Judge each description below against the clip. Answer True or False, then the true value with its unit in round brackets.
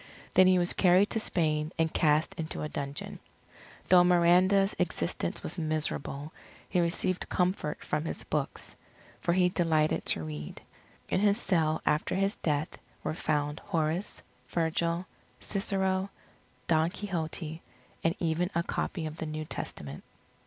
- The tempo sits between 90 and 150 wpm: True (140 wpm)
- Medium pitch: True (165 Hz)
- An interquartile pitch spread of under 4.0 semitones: True (2.9 semitones)